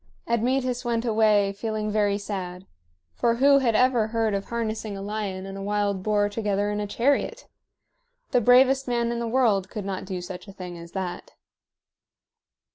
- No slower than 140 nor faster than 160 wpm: No, average, 175 wpm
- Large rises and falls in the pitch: No, average, 3.1 semitones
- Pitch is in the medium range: No, high, 215 Hz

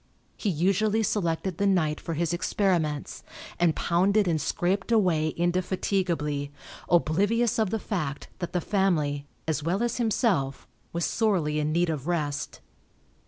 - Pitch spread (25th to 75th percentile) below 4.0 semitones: No, average, 4.3 semitones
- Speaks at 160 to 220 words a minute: No, average, 140 wpm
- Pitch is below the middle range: No, medium, 175 Hz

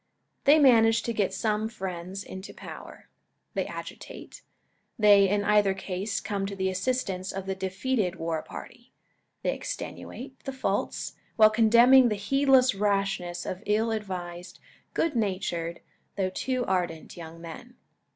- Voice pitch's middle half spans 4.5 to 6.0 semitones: No, average, 3.7 semitones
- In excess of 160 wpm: No, average, 140 wpm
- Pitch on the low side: No, high, 200 Hz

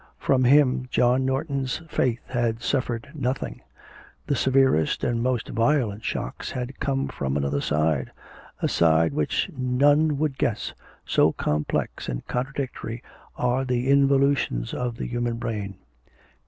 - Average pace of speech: No, slow, 130 wpm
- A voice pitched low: Yes, low, 125 Hz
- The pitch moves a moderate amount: Yes, average, 3.4 semitones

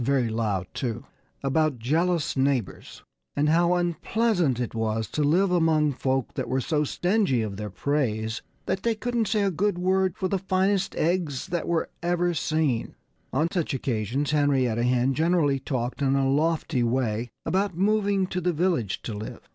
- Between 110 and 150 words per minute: No, average, 170 wpm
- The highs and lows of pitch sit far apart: Yes, wide, 6.2 semitones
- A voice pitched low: No, medium, 150 Hz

